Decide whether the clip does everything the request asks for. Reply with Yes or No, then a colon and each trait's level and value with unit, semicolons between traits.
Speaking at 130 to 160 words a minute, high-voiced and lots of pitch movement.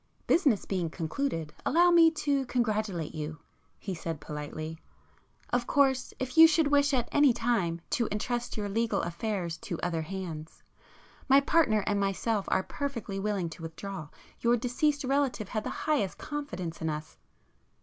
Yes: average, 150 wpm; high, 210 Hz; wide, 8.1 semitones